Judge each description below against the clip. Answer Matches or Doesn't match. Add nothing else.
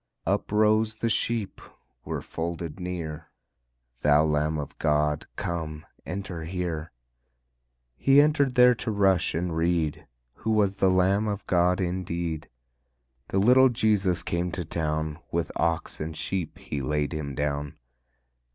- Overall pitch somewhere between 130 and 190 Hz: Doesn't match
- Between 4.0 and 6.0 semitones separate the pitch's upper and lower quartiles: Matches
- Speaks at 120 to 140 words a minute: Matches